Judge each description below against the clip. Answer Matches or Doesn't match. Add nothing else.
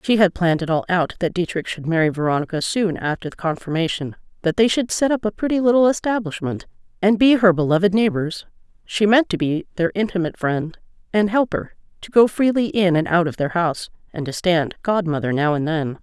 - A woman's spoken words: Matches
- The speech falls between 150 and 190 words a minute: Doesn't match